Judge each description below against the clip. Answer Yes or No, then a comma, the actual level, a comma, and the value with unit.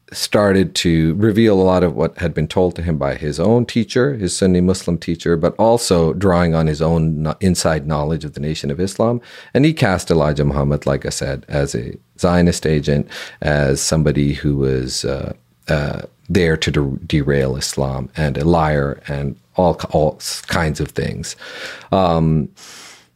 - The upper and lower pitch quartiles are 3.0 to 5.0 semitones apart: Yes, average, 3.9 semitones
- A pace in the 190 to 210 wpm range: No, average, 170 wpm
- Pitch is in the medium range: No, very low, 80 Hz